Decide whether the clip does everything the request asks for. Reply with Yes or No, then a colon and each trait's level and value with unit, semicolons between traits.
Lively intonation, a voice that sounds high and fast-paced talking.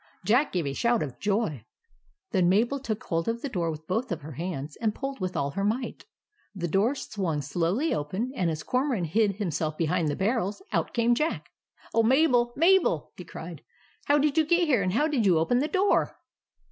Yes: wide, 7.4 semitones; high, 210 Hz; fast, 210 wpm